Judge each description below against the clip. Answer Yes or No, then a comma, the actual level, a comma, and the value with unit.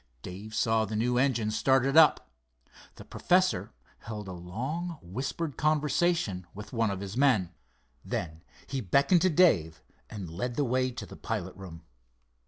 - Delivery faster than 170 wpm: No, average, 155 wpm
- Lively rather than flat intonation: Yes, wide, 6.5 semitones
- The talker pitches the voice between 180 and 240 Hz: No, low, 115 Hz